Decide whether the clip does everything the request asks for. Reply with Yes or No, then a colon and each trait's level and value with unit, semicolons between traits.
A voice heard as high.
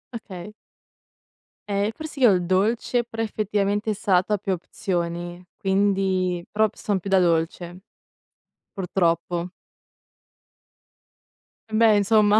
Yes: high, 195 Hz